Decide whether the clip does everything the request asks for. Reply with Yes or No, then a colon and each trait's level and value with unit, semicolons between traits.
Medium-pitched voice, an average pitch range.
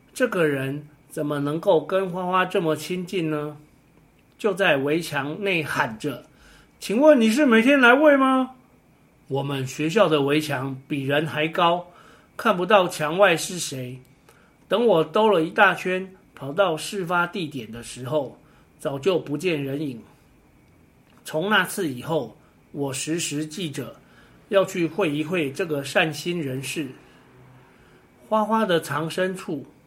Yes: medium, 160 Hz; average, 4.8 semitones